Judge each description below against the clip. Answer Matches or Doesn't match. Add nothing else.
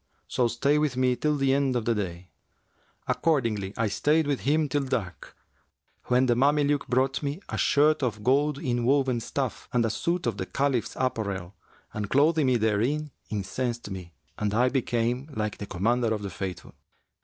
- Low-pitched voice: Matches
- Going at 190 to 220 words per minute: Doesn't match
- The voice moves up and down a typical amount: Matches